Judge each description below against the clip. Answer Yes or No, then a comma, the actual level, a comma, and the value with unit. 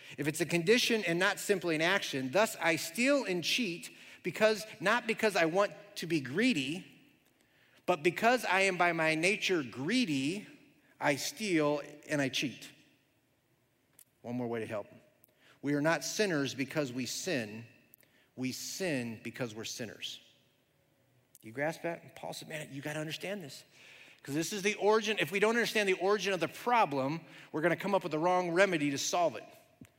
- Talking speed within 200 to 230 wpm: No, average, 175 wpm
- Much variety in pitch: Yes, wide, 6.4 semitones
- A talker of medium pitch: Yes, medium, 165 Hz